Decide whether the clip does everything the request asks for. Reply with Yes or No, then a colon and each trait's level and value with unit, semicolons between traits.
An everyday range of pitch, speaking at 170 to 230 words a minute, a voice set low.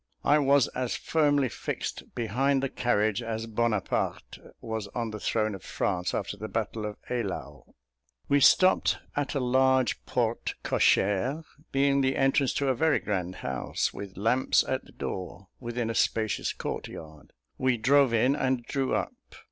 No: average, 4.0 semitones; average, 160 wpm; low, 120 Hz